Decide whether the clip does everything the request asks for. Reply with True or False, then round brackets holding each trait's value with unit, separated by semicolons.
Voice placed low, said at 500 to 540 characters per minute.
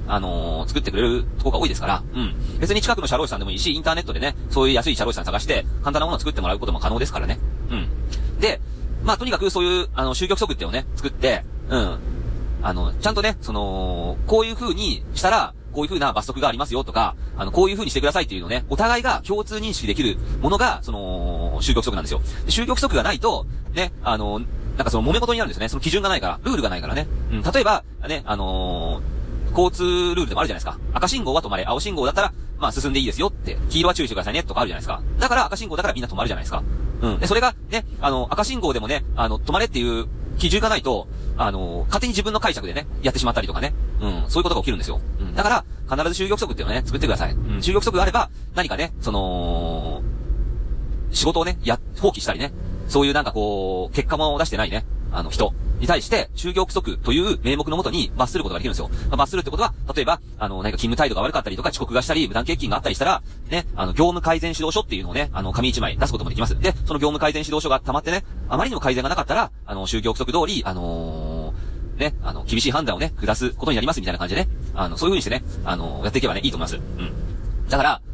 True (125 Hz; 515 characters per minute)